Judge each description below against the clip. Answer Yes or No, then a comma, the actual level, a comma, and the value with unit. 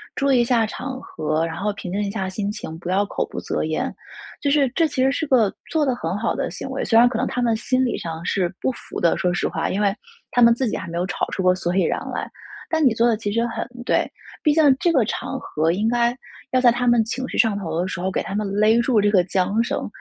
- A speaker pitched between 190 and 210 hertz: No, high, 225 Hz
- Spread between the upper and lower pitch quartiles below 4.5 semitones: No, average, 5.1 semitones